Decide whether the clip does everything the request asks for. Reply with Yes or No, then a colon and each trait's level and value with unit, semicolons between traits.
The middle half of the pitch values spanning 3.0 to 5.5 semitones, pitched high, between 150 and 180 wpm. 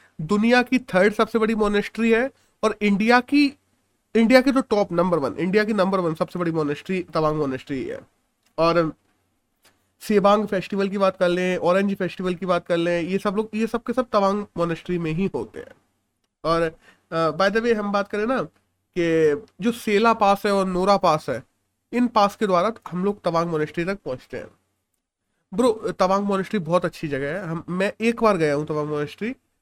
No: average, 4.2 semitones; high, 195 Hz; fast, 190 wpm